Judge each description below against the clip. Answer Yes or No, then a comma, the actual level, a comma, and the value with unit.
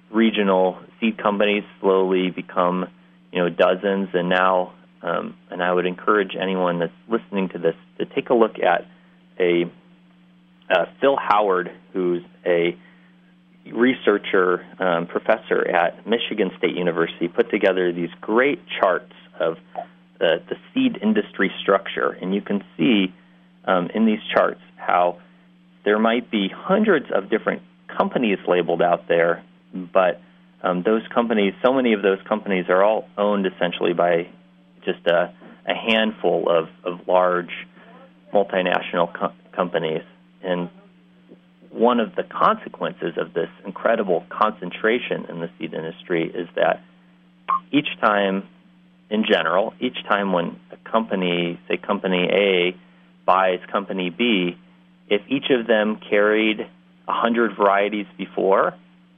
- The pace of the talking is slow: Yes, slow, 130 wpm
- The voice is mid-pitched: No, very low, 90 Hz